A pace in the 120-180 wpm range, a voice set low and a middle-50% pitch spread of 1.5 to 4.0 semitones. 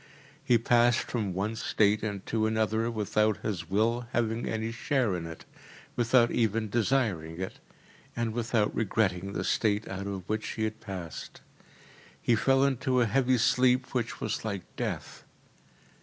Yes: average, 150 wpm; low, 110 Hz; average, 2.9 semitones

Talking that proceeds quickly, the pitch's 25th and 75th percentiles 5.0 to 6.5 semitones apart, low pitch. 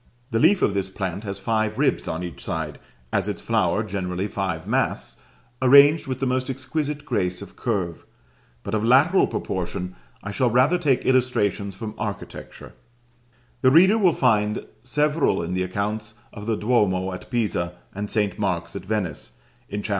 No: average, 170 wpm; wide, 5.4 semitones; low, 105 Hz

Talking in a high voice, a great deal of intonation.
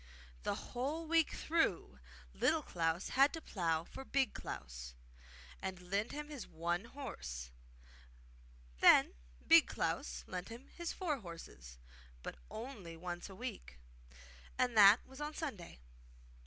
Yes: high, 205 Hz; wide, 8.7 semitones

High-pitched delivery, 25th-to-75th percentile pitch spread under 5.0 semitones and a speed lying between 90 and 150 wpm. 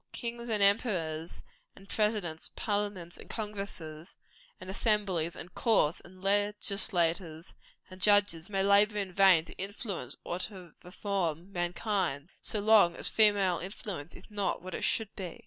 Yes: high, 195 Hz; average, 3.2 semitones; average, 145 wpm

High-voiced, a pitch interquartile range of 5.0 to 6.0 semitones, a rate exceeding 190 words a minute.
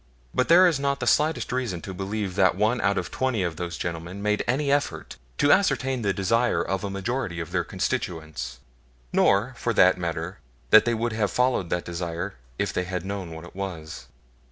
No: low, 100 Hz; wide, 5.6 semitones; average, 200 wpm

